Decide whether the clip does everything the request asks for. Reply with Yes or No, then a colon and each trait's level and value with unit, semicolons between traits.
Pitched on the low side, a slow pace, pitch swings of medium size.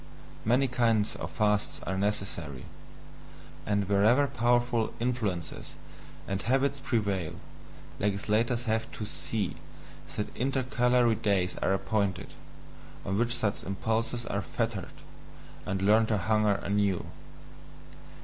Yes: low, 110 Hz; slow, 110 wpm; average, 3.3 semitones